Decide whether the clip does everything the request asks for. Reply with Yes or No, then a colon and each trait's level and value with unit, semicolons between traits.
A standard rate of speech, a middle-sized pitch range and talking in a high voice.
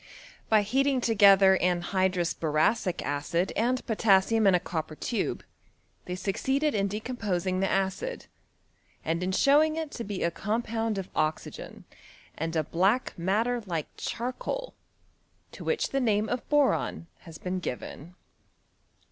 Yes: average, 145 wpm; average, 5.0 semitones; high, 195 Hz